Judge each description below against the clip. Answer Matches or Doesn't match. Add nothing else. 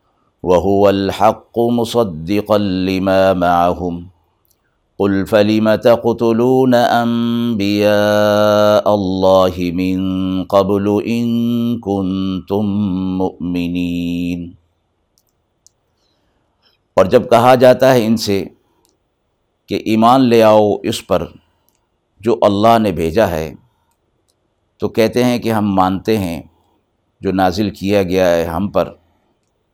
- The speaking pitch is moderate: Doesn't match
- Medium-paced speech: Doesn't match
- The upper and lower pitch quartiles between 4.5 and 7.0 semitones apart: Doesn't match